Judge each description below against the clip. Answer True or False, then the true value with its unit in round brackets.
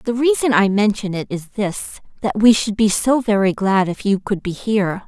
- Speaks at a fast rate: True (225 wpm)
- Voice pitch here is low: False (205 Hz)